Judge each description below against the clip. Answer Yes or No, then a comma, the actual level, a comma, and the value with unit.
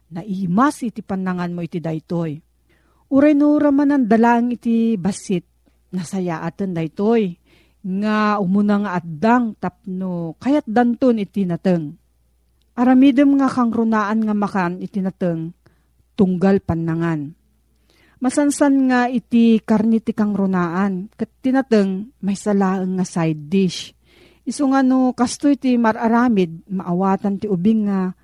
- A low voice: No, high, 205 Hz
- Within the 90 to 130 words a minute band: Yes, average, 120 wpm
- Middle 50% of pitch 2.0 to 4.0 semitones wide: No, average, 4.6 semitones